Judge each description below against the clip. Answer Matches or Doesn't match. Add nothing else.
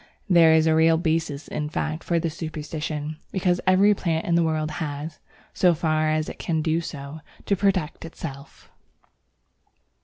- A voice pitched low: Doesn't match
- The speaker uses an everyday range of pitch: Doesn't match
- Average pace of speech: Matches